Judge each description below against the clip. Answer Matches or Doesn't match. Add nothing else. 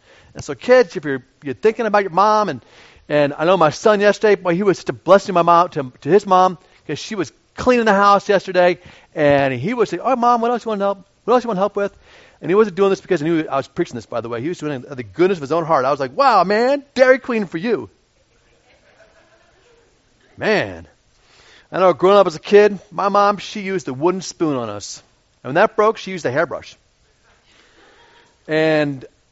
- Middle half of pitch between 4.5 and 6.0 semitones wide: Matches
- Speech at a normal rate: Doesn't match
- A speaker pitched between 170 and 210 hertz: Matches